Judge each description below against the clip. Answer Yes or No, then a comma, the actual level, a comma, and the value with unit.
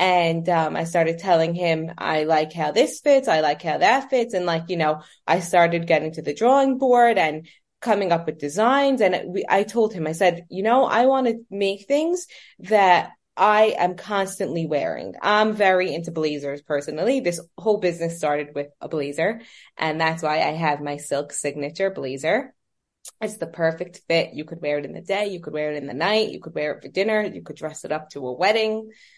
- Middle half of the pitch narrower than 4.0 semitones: No, wide, 5.4 semitones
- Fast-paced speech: Yes, fast, 215 wpm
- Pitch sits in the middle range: Yes, medium, 170 Hz